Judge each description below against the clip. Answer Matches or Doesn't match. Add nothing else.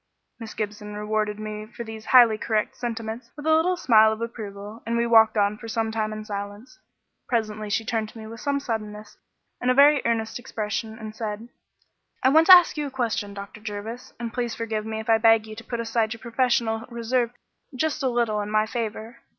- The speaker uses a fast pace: Matches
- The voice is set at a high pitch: Matches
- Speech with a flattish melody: Matches